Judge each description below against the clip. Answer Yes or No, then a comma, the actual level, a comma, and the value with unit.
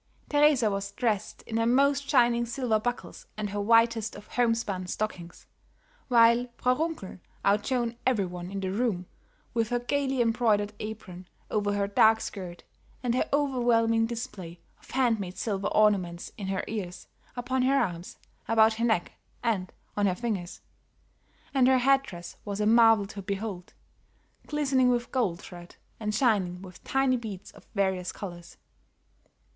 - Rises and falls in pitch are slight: No, average, 3.8 semitones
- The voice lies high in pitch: Yes, high, 220 Hz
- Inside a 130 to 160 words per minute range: Yes, average, 155 wpm